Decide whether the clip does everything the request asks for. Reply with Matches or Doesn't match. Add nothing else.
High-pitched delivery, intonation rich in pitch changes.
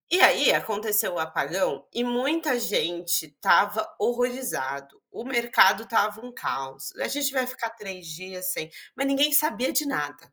Matches